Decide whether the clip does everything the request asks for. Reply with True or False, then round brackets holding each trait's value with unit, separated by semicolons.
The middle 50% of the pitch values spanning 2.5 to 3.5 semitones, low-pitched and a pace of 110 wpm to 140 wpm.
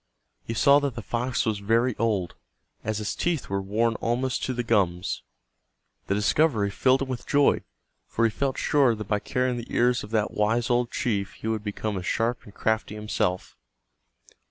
False (3.1 semitones; 115 Hz; 185 wpm)